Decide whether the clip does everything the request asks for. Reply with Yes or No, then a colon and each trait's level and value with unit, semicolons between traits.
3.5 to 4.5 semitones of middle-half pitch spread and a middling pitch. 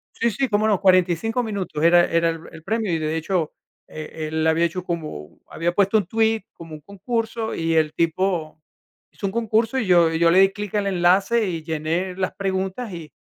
Yes: average, 4.2 semitones; medium, 180 Hz